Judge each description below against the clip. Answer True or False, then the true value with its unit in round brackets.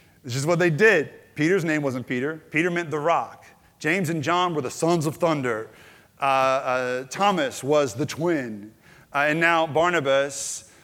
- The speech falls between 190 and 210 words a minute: False (170 wpm)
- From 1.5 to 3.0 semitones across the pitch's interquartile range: False (4.1 semitones)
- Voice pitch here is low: False (155 Hz)